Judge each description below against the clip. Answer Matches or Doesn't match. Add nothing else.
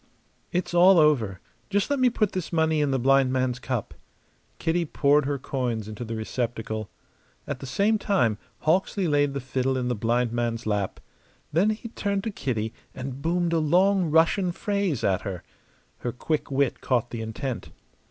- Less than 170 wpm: Doesn't match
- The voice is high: Doesn't match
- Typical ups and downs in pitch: Doesn't match